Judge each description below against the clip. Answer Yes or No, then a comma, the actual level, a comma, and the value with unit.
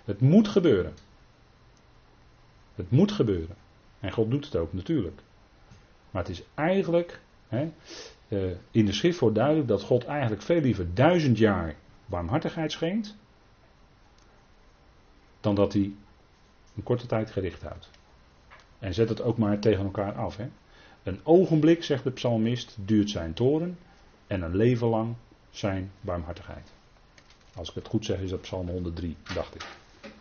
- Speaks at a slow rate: No, average, 145 wpm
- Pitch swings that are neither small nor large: No, wide, 5.8 semitones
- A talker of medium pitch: No, low, 110 Hz